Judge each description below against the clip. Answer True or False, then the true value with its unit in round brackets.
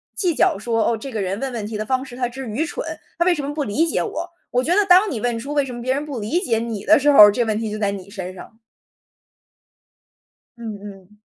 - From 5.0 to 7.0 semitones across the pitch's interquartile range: True (5.3 semitones)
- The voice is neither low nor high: False (245 Hz)